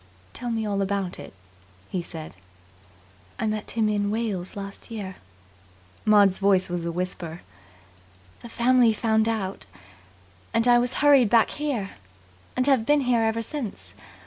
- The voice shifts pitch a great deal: No, average, 3.4 semitones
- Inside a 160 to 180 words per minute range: No, average, 145 wpm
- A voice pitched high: Yes, high, 215 Hz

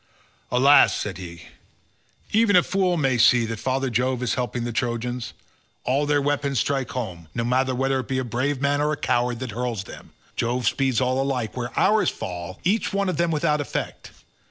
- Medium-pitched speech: No, low, 130 Hz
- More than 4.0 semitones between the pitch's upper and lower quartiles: No, average, 3.2 semitones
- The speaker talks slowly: No, average, 195 wpm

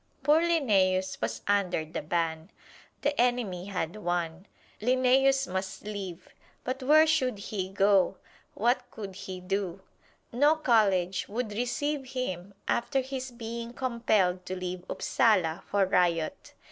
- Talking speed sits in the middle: No, slow, 130 wpm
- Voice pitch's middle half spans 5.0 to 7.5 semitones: Yes, wide, 5.6 semitones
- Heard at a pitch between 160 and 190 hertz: No, high, 205 Hz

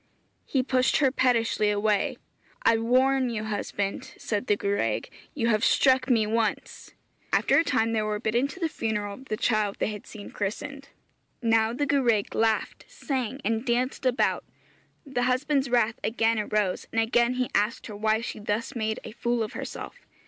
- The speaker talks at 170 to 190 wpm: Yes, average, 175 wpm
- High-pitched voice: Yes, high, 230 Hz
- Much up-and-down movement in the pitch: No, average, 3.0 semitones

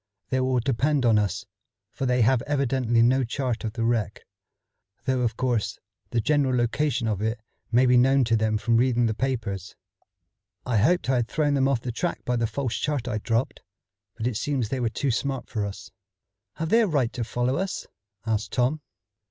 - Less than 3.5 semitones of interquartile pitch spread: Yes, average, 2.9 semitones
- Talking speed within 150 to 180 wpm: No, average, 200 wpm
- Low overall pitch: Yes, low, 125 Hz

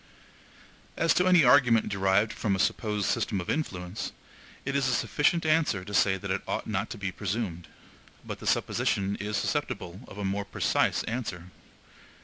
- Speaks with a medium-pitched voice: No, low, 105 Hz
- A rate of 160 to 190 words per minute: Yes, average, 170 wpm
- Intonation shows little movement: No, average, 4.4 semitones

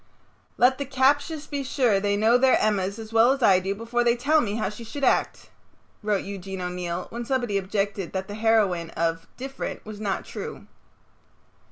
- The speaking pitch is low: No, high, 215 Hz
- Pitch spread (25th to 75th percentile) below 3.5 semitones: No, average, 4.2 semitones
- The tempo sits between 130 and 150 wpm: No, average, 185 wpm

